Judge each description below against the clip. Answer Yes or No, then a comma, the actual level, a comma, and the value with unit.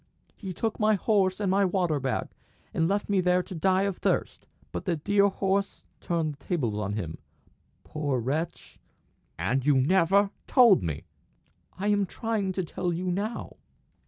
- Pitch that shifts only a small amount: No, average, 4.8 semitones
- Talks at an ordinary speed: Yes, average, 165 wpm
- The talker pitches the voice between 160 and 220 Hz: Yes, medium, 185 Hz